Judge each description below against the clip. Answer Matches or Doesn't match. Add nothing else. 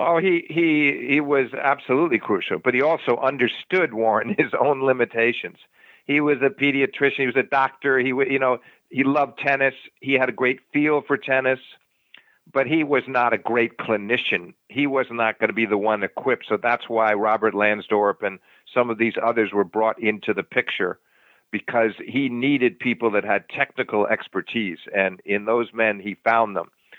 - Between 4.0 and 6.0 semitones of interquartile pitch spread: Doesn't match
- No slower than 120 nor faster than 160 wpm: Doesn't match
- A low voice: Matches